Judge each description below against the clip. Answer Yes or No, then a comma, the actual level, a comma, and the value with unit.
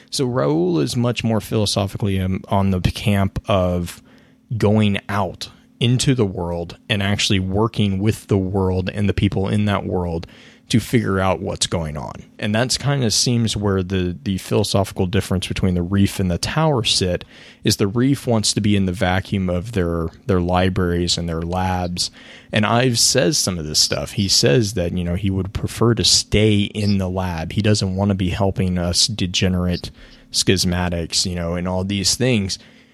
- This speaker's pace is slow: No, average, 185 wpm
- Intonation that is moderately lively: Yes, average, 3.3 semitones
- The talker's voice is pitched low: Yes, low, 100 Hz